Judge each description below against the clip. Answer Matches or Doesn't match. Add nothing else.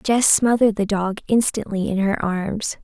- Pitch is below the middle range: Doesn't match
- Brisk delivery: Doesn't match